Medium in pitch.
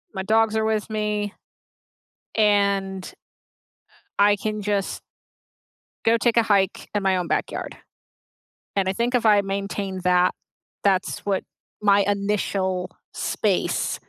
No: high, 200 Hz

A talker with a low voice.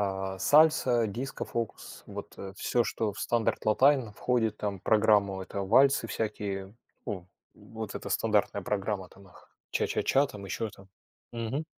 Yes: low, 105 Hz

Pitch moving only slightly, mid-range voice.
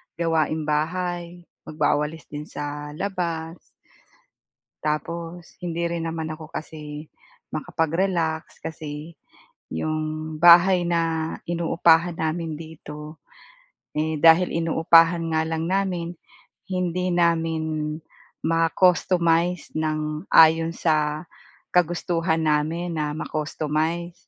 Yes: narrow, 1.6 semitones; medium, 165 Hz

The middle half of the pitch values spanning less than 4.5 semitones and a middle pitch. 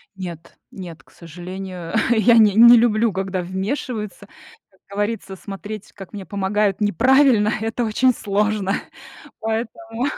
No: average, 2.9 semitones; high, 210 Hz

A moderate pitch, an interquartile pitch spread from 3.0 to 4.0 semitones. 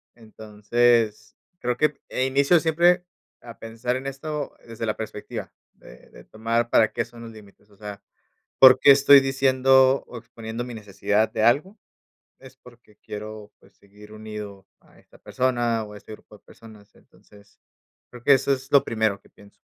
No: low, 115 Hz; average, 3.7 semitones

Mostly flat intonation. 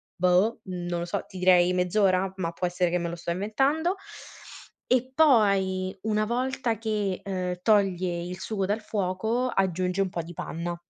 No: average, 3.2 semitones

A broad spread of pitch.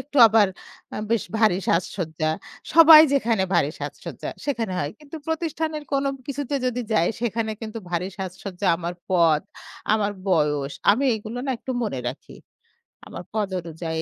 Yes: wide, 7.2 semitones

